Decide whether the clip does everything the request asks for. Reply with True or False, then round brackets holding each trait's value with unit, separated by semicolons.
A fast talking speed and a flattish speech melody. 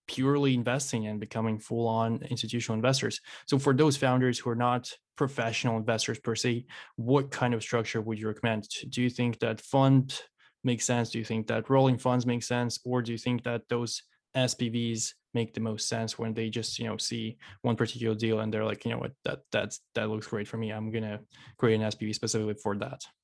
True (210 wpm; 1.9 semitones)